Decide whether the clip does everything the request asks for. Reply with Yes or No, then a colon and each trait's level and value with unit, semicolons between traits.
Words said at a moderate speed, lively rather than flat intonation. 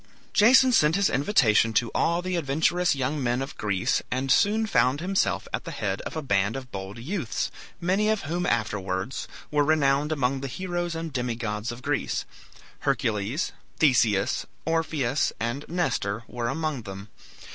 Yes: average, 155 wpm; wide, 6.3 semitones